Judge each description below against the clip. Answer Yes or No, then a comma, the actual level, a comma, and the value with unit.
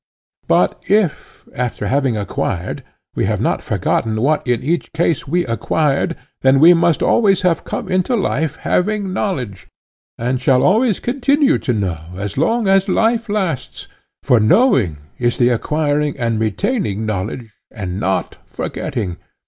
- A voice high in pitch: No, medium, 140 Hz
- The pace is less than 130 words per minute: No, average, 140 wpm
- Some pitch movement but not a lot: No, wide, 8.9 semitones